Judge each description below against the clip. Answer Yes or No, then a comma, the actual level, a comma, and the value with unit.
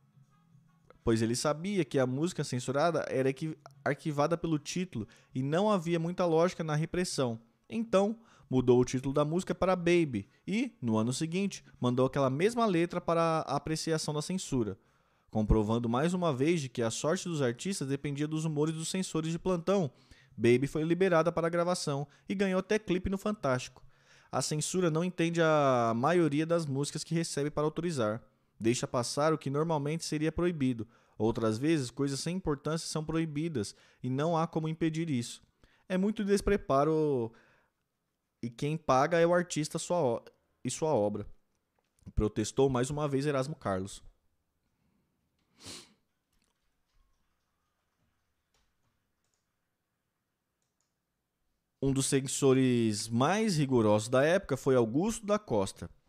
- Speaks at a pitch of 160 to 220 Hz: No, medium, 150 Hz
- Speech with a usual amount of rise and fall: Yes, average, 4.9 semitones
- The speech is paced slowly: No, average, 140 wpm